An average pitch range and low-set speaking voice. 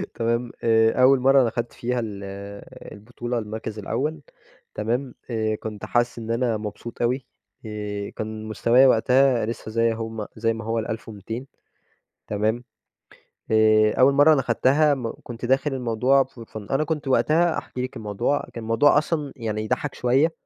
Yes: average, 3.1 semitones; low, 115 Hz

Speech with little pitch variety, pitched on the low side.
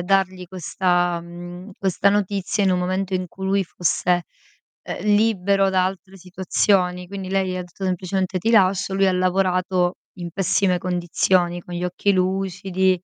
No: narrow, 1.4 semitones; medium, 185 Hz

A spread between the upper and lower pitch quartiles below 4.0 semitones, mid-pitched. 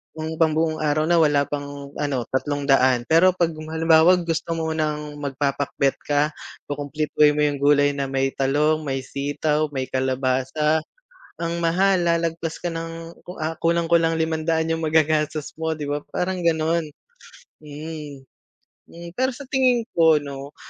Yes: narrow, 2.4 semitones; medium, 155 Hz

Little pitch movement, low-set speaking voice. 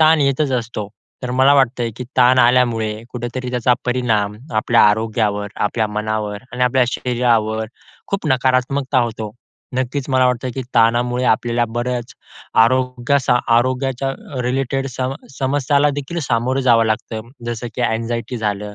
Yes: narrow, 2.3 semitones; low, 125 Hz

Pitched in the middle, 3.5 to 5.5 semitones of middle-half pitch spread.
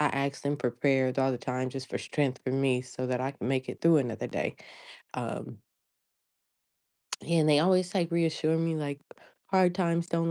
Yes: medium, 145 Hz; average, 4.4 semitones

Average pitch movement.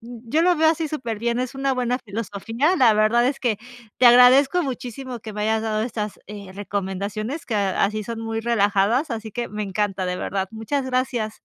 Yes: average, 3.3 semitones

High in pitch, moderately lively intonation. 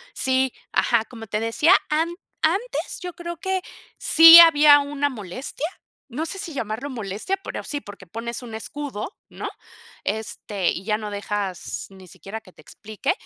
No: high, 245 Hz; wide, 6.4 semitones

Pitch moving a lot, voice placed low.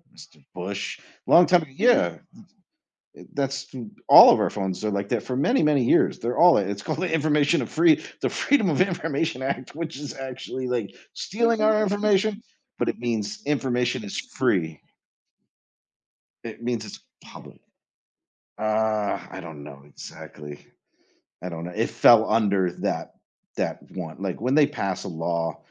Yes: wide, 8.2 semitones; low, 120 Hz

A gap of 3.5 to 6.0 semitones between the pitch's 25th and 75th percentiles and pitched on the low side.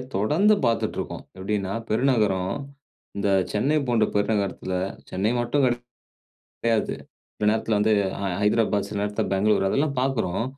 No: average, 2.9 semitones; low, 105 Hz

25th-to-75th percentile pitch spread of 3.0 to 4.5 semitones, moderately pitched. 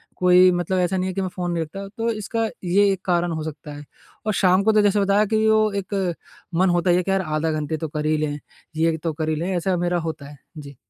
Yes: average, 3.6 semitones; medium, 180 Hz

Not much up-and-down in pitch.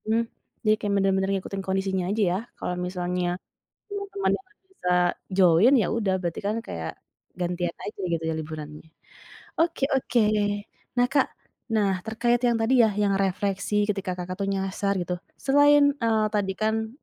No: average, 4.0 semitones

